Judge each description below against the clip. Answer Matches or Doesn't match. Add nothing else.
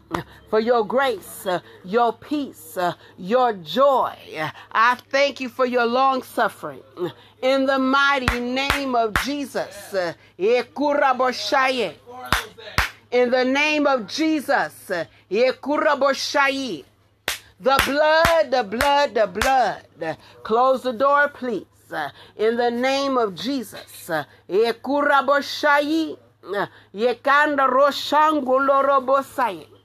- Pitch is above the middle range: Matches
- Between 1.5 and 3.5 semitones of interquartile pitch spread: Matches